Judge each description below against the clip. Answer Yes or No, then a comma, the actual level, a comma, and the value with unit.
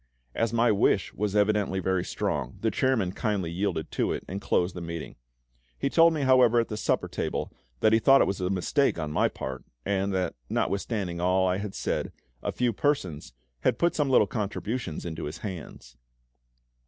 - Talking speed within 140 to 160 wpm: No, average, 190 wpm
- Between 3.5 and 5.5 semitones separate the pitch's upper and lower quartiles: Yes, average, 4.5 semitones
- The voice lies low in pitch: Yes, low, 100 Hz